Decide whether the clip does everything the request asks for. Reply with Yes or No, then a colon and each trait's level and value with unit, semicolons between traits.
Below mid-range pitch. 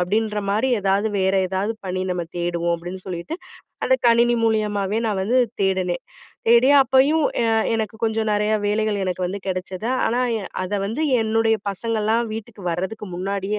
No: high, 210 Hz